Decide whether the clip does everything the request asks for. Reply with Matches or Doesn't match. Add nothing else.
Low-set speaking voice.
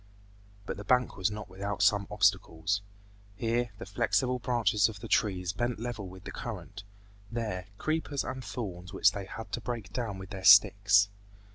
Matches